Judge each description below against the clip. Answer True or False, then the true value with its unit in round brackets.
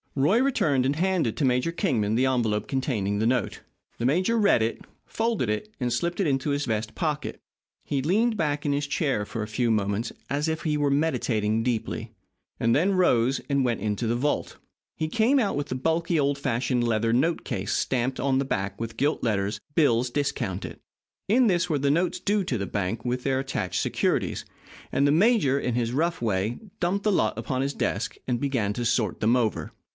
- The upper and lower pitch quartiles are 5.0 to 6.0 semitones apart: True (5.6 semitones)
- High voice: False (135 Hz)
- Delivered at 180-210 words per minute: True (200 wpm)